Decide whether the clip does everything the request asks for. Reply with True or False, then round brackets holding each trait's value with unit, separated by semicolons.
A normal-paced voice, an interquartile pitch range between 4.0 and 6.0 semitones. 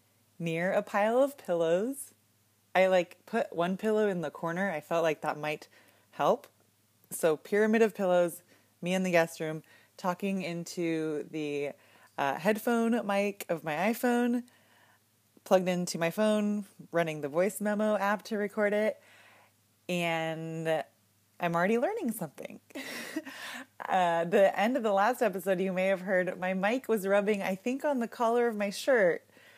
True (155 wpm; 4.4 semitones)